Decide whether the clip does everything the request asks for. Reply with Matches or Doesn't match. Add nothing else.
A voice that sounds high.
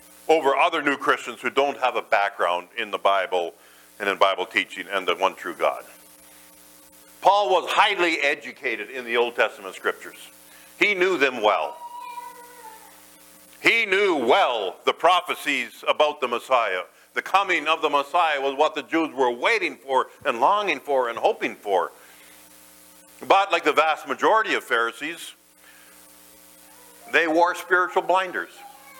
Doesn't match